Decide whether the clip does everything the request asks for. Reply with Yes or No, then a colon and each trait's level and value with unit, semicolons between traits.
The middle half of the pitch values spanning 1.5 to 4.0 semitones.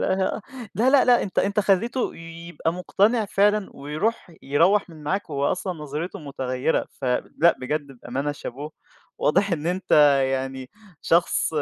No: wide, 5.4 semitones